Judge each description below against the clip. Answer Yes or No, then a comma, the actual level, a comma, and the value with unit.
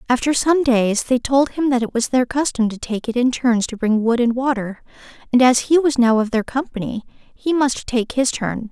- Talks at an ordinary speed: No, fast, 235 wpm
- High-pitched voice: Yes, high, 245 Hz